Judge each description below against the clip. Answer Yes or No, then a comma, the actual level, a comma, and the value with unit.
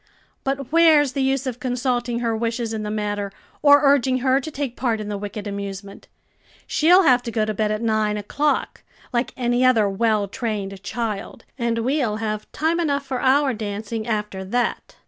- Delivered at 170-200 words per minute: Yes, average, 185 wpm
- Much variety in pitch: No, average, 4.0 semitones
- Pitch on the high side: Yes, high, 235 Hz